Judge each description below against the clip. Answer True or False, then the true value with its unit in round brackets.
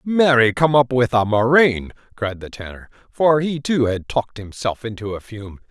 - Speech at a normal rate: True (190 wpm)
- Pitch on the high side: False (120 Hz)